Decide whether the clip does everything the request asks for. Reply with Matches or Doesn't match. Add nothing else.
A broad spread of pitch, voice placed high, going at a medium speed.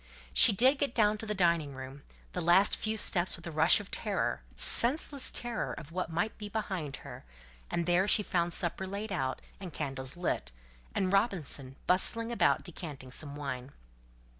Doesn't match